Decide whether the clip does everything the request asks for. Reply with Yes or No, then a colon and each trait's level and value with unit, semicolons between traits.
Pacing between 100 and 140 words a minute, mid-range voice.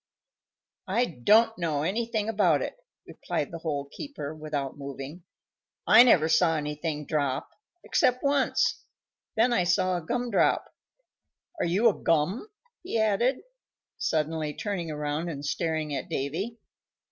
Yes: slow, 135 wpm; medium, 165 Hz